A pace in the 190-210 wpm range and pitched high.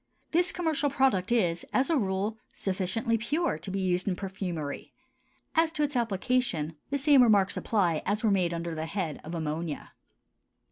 No: average, 170 wpm; high, 195 Hz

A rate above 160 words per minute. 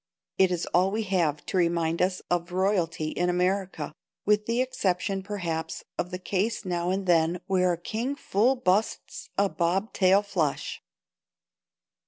No: average, 155 wpm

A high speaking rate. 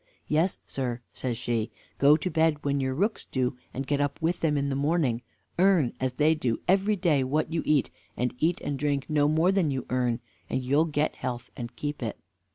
Yes: fast, 210 wpm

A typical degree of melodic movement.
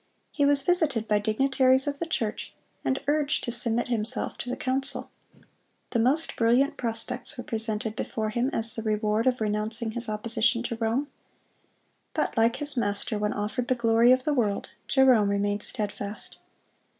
Yes: average, 3.3 semitones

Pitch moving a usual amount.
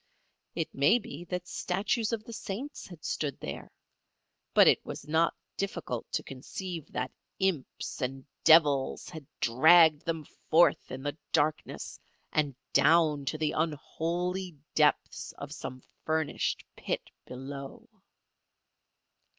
Yes: average, 3.8 semitones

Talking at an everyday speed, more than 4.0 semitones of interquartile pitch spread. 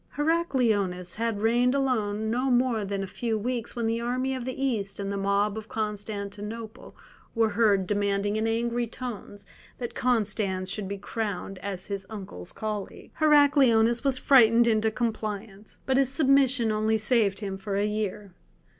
No: average, 160 wpm; average, 3.1 semitones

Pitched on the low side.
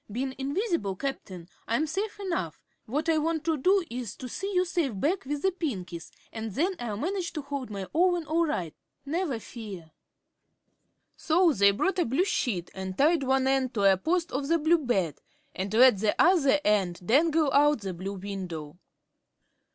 No: very high, 270 Hz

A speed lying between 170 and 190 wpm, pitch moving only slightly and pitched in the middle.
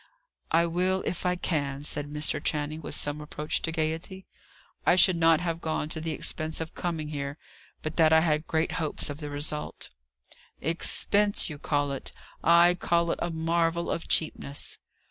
Yes: average, 175 wpm; narrow, 2.1 semitones; medium, 160 Hz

